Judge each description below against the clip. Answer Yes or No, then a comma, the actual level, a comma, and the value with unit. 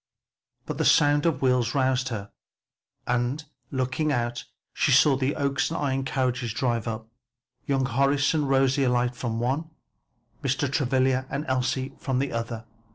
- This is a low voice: Yes, low, 130 Hz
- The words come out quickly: No, average, 160 wpm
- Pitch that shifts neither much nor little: No, narrow, 2.2 semitones